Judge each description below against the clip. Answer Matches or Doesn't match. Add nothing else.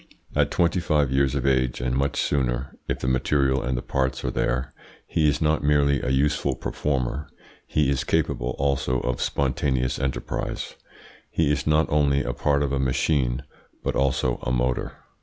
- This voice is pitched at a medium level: Doesn't match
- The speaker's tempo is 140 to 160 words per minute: Doesn't match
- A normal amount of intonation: Doesn't match